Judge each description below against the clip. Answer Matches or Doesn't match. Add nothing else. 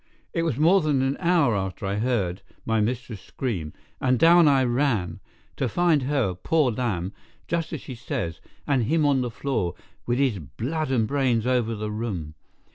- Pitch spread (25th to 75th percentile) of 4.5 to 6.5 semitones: Matches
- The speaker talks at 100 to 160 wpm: Doesn't match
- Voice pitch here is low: Matches